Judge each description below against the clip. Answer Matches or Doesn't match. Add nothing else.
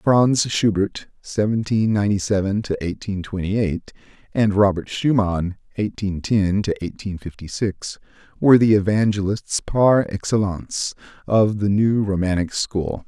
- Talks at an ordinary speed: Doesn't match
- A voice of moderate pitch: Doesn't match